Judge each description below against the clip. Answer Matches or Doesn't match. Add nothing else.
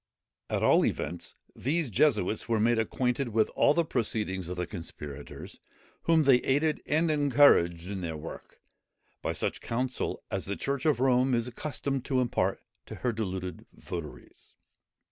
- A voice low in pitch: Matches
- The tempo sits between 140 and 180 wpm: Matches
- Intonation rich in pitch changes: Matches